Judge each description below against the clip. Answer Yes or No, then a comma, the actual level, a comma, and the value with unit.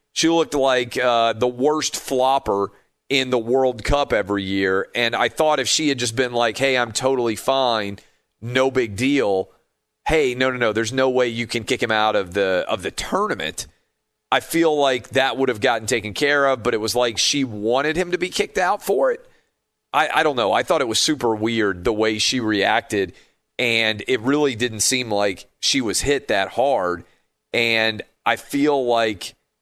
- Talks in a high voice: No, low, 125 Hz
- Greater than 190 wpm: Yes, average, 200 wpm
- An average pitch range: Yes, average, 3.5 semitones